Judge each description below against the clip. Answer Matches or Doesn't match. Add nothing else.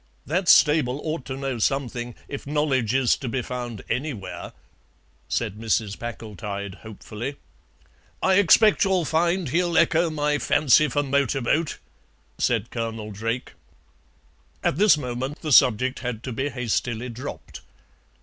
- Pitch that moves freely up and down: Doesn't match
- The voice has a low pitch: Matches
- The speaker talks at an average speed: Doesn't match